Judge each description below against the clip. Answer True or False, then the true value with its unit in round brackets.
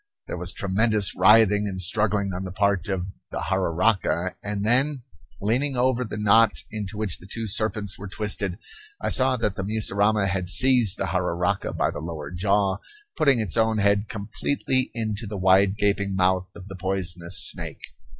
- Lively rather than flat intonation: False (2.7 semitones)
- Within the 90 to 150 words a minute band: False (170 wpm)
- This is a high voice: False (100 Hz)